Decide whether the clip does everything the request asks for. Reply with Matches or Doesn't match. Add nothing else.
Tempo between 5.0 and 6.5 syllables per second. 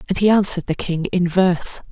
Matches